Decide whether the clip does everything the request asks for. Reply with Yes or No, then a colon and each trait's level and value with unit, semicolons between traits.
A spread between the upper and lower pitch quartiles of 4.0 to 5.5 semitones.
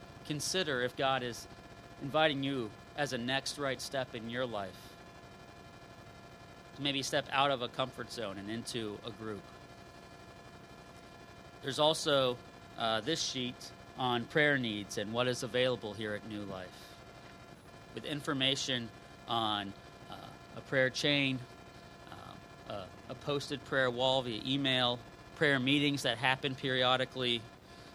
No: average, 3.1 semitones